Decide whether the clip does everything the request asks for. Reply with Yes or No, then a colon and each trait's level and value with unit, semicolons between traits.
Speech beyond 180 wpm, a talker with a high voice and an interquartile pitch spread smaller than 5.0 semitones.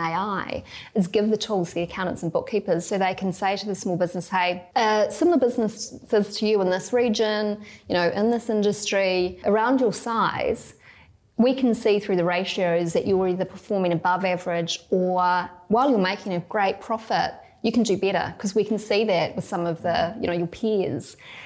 Yes: average, 200 wpm; high, 195 Hz; average, 3.2 semitones